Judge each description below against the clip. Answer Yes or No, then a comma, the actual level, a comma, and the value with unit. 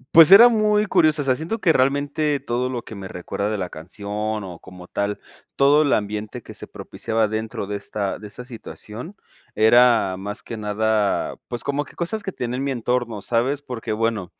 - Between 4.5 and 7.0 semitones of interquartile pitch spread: Yes, wide, 5.5 semitones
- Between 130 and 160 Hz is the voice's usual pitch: No, low, 115 Hz